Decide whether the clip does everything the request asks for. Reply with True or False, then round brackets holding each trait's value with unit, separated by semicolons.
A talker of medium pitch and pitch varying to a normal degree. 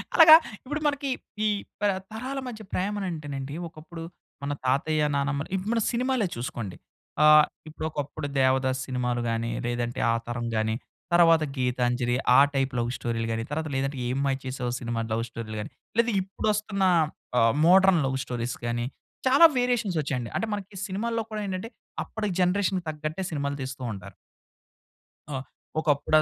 False (145 Hz; 7.8 semitones)